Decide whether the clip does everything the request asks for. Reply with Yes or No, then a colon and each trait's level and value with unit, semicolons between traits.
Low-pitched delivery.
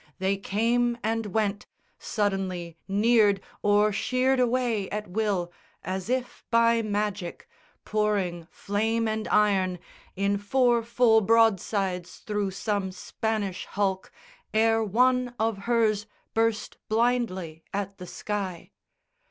No: high, 210 Hz